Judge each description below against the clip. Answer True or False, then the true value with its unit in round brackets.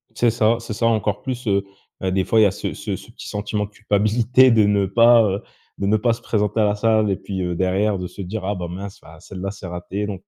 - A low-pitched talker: True (105 Hz)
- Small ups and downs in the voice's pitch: True (2.3 semitones)